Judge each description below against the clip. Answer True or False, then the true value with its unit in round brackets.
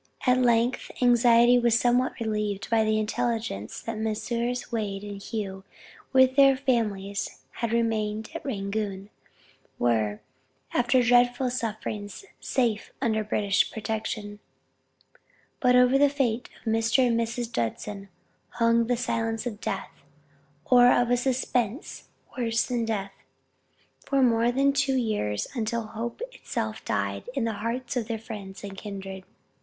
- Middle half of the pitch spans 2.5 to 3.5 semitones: True (2.8 semitones)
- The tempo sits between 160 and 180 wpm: False (140 wpm)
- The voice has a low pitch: False (230 Hz)